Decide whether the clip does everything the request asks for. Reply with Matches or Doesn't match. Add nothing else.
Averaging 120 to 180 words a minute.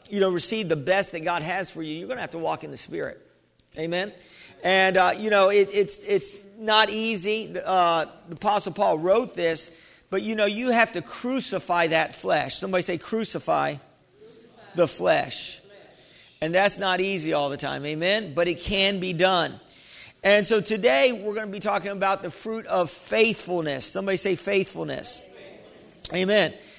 Matches